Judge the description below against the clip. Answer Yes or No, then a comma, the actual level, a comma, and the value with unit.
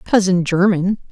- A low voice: No, medium, 185 Hz